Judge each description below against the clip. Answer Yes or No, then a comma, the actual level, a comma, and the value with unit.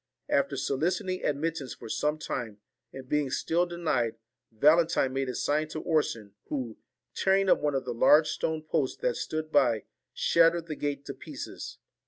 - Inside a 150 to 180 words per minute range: Yes, average, 175 wpm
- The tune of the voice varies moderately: Yes, average, 3.7 semitones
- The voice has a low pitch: No, medium, 150 Hz